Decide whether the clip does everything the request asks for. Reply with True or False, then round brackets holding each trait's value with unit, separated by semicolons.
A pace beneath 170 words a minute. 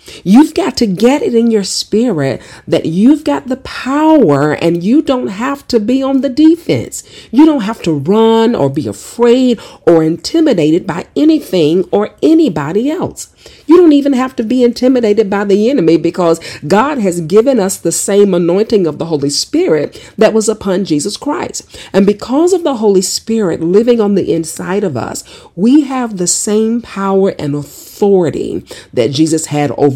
False (175 wpm)